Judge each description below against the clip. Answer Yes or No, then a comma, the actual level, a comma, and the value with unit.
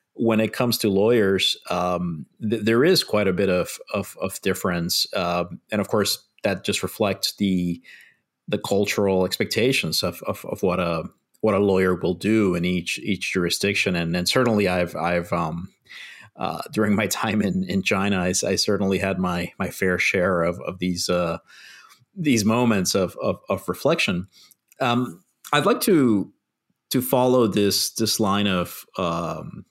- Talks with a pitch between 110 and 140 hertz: No, very low, 95 Hz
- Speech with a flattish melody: No, average, 3.6 semitones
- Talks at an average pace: Yes, average, 170 wpm